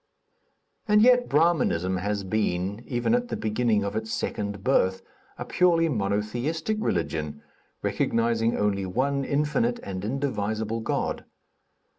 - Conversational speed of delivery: No, slow, 120 wpm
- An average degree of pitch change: No, wide, 6.7 semitones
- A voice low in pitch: Yes, low, 110 Hz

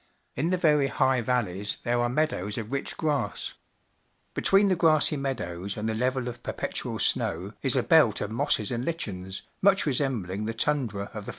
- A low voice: Yes, low, 125 Hz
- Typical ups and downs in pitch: No, wide, 5.9 semitones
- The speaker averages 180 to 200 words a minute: Yes, average, 185 wpm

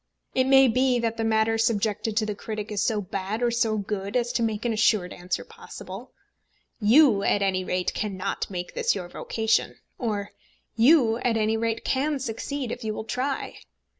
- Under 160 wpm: No, average, 185 wpm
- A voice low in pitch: No, high, 220 Hz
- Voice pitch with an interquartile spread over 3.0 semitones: No, average, 2.7 semitones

